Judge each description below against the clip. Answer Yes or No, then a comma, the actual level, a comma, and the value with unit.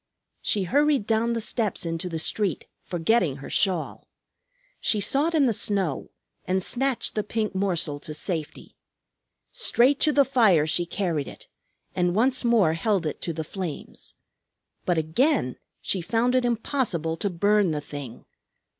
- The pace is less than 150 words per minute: No, average, 155 wpm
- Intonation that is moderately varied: No, wide, 6.3 semitones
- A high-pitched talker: Yes, high, 195 Hz